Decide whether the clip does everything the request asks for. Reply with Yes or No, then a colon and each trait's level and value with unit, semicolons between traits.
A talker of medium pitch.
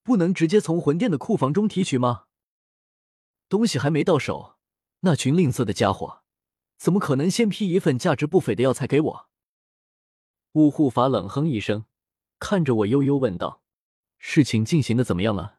Yes: medium, 145 Hz